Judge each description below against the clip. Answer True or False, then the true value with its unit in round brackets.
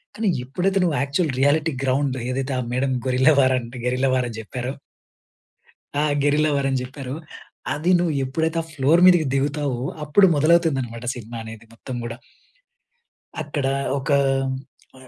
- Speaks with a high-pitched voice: False (135 Hz)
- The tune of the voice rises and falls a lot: False (3.3 semitones)